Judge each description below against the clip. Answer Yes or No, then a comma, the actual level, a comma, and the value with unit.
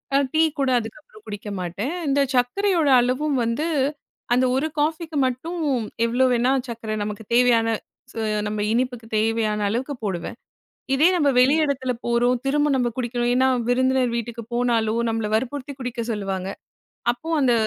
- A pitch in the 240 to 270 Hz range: Yes, high, 245 Hz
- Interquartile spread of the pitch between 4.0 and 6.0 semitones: No, average, 3.2 semitones